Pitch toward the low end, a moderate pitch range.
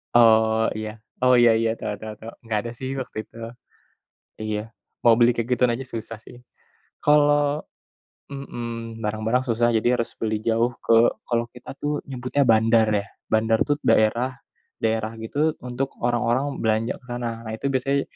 No: low, 115 Hz; narrow, 2.3 semitones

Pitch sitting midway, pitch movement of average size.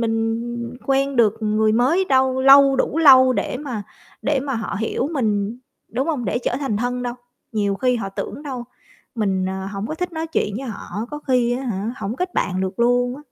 No: high, 245 Hz; average, 4.0 semitones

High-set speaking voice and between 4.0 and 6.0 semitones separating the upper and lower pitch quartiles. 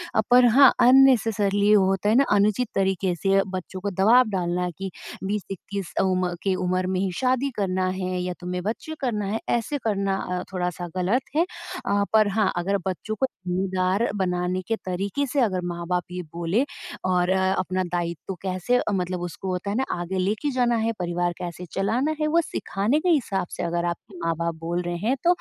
No: high, 195 Hz; average, 3.3 semitones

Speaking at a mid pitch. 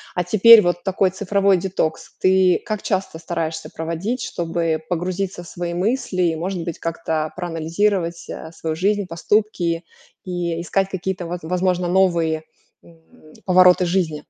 Yes: medium, 180 Hz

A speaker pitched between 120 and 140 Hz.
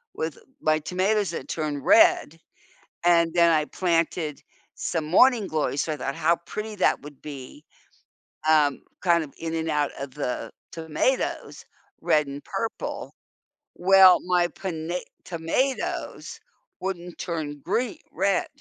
No: medium, 165 Hz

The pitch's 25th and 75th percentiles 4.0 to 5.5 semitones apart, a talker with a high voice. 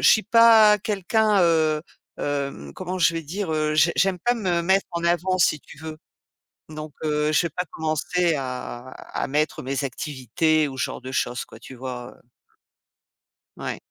No: average, 4.6 semitones; medium, 155 Hz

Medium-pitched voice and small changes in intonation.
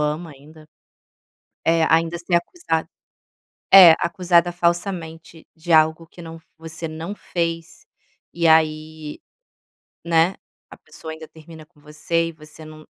Yes: medium, 165 Hz; narrow, 1.4 semitones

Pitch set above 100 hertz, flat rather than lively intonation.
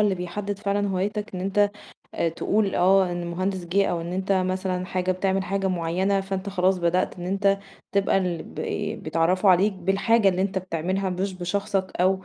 Yes: high, 190 Hz; narrow, 1.5 semitones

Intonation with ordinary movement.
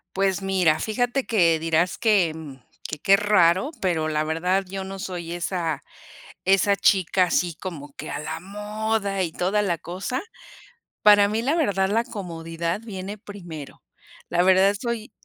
Yes: average, 3.6 semitones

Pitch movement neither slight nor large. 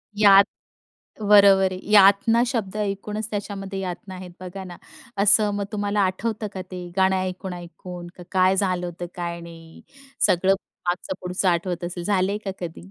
No: narrow, 2.1 semitones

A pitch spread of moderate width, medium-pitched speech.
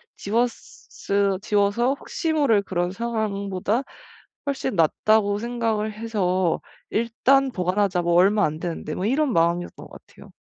No: average, 4.2 semitones; high, 205 Hz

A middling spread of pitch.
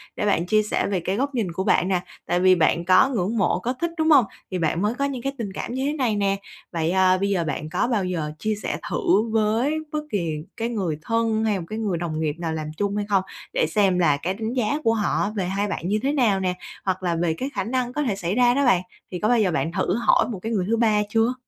Yes: average, 4.4 semitones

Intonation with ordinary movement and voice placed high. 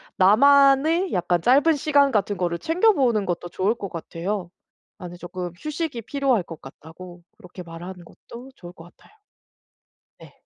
No: wide, 7.9 semitones; high, 200 Hz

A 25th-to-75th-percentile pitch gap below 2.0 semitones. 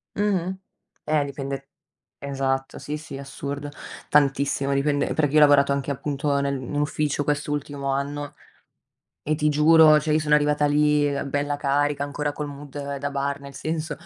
Yes: narrow, 1.2 semitones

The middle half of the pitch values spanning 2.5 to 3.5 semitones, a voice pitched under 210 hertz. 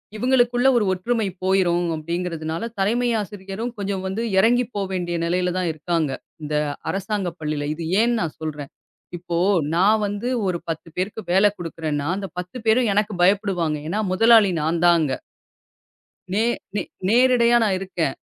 No: average, 4.2 semitones; high, 190 Hz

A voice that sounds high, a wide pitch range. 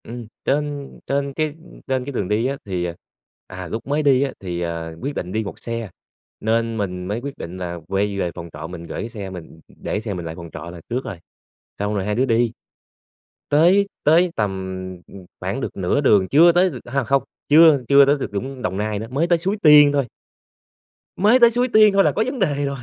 No: low, 120 Hz; wide, 7.1 semitones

